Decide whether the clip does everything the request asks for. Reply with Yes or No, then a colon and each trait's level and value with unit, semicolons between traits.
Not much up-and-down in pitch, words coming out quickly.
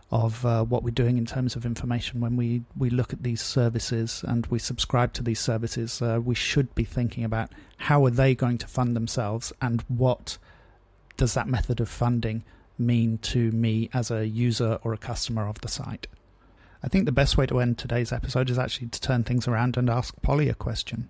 Yes: narrow, 1.6 semitones; fast, 210 wpm